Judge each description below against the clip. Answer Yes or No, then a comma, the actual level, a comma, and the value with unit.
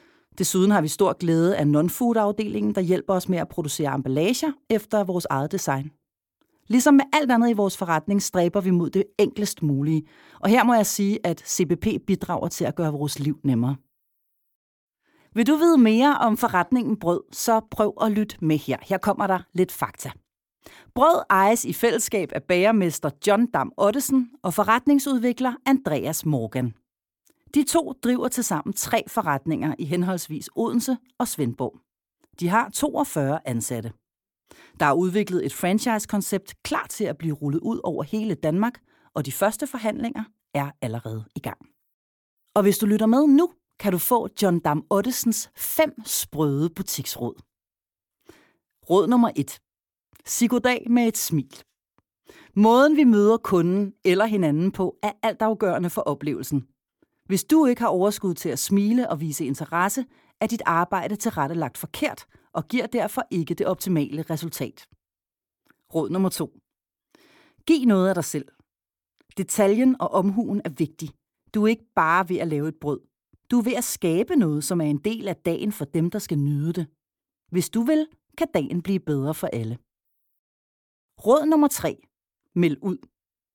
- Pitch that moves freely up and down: Yes, wide, 6.6 semitones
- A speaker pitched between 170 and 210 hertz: Yes, high, 190 Hz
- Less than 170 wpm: Yes, average, 160 wpm